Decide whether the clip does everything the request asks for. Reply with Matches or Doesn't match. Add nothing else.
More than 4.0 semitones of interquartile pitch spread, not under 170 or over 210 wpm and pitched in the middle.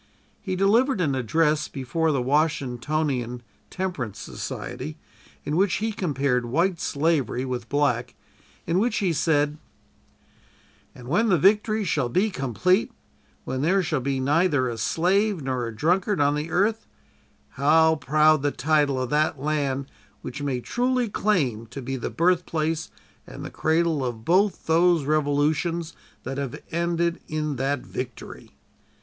Doesn't match